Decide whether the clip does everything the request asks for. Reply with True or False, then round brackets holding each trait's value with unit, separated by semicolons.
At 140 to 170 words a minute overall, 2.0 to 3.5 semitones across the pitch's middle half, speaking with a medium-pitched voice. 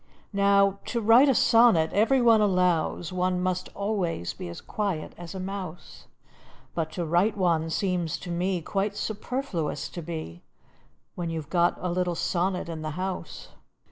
True (165 wpm; 3.0 semitones; 180 Hz)